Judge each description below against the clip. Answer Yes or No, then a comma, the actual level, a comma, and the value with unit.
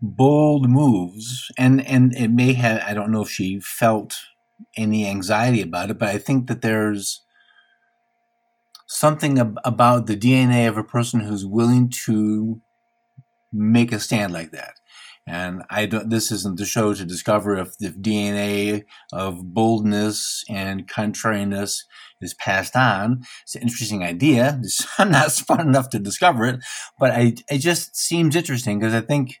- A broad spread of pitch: No, average, 3.9 semitones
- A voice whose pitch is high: No, low, 115 Hz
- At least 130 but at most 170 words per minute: Yes, average, 155 wpm